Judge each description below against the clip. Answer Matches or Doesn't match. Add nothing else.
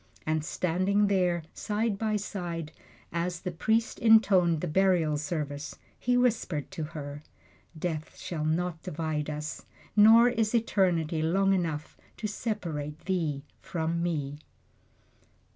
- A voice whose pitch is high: Doesn't match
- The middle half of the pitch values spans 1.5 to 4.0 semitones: Doesn't match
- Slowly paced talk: Matches